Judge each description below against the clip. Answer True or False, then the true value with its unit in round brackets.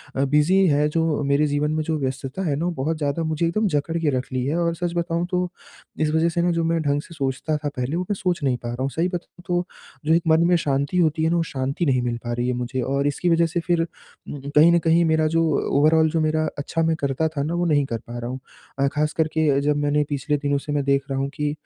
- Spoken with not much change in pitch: False (3.0 semitones)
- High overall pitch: False (155 Hz)